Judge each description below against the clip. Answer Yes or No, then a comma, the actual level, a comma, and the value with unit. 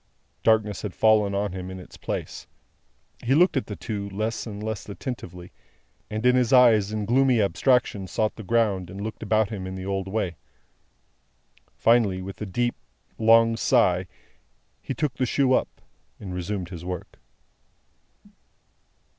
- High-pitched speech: No, low, 105 Hz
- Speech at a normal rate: Yes, average, 155 wpm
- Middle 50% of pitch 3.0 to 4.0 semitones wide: Yes, average, 3.3 semitones